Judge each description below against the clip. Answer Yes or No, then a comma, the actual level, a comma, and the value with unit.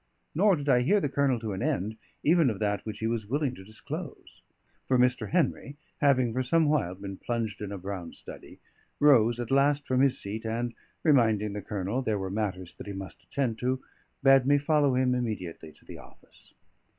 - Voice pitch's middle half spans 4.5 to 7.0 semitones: Yes, average, 5.0 semitones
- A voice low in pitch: Yes, low, 120 Hz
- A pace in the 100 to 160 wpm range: No, average, 200 wpm